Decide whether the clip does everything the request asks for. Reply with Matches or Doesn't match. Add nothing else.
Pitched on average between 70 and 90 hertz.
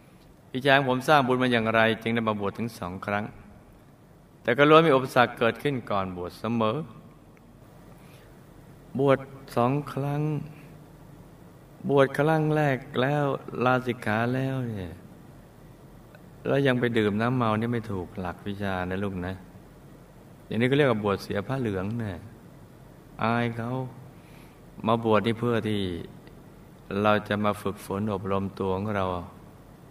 Doesn't match